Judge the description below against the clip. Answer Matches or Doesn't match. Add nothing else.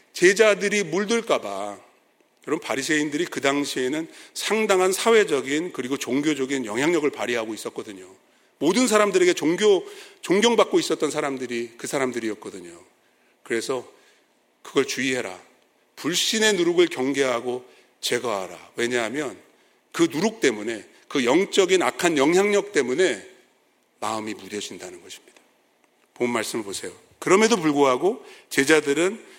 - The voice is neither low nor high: Matches